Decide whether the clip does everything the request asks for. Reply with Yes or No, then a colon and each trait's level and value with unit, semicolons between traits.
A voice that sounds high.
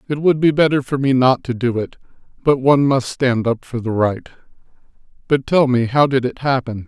No: low, 130 Hz